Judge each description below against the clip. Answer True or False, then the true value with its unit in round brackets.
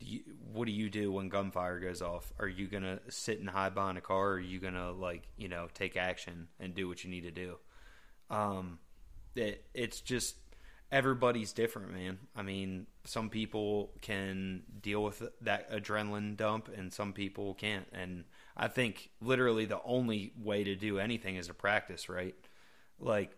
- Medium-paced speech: True (180 wpm)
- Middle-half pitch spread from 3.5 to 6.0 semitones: False (2.7 semitones)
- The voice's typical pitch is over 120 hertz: False (100 Hz)